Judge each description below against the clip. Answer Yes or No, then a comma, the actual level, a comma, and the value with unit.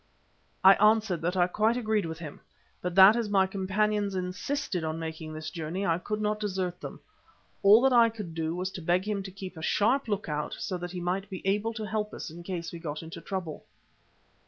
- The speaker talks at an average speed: No, fast, 220 wpm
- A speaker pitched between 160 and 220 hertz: Yes, high, 190 Hz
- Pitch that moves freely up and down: No, average, 3.5 semitones